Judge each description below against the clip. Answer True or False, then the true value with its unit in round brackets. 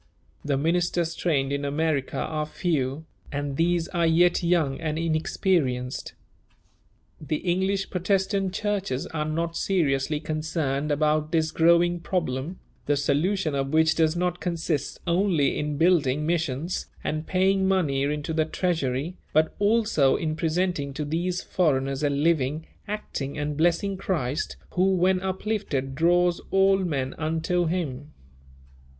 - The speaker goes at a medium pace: False (130 wpm)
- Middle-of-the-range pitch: True (160 Hz)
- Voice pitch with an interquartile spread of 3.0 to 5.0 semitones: True (3.6 semitones)